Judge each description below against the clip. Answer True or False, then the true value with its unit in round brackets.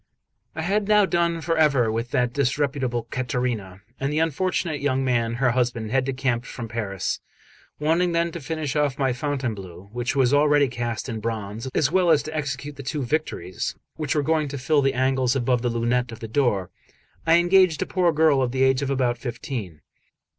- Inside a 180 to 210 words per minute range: True (195 wpm)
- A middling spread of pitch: True (4.2 semitones)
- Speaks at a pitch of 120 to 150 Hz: True (135 Hz)